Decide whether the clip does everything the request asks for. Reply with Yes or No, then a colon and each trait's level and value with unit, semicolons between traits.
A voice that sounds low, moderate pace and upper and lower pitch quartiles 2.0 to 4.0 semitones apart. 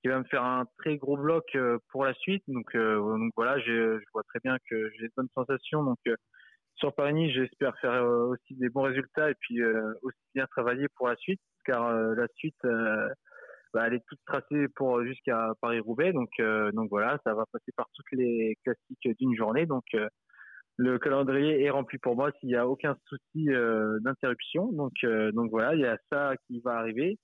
Yes: low, 125 Hz; average, 210 wpm; average, 3.2 semitones